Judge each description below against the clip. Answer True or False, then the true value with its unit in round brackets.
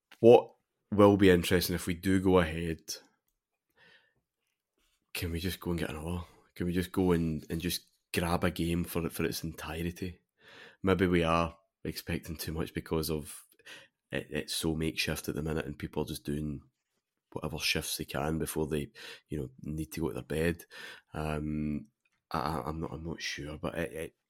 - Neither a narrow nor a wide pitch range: False (2.1 semitones)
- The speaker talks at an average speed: True (185 wpm)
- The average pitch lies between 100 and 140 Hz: False (80 Hz)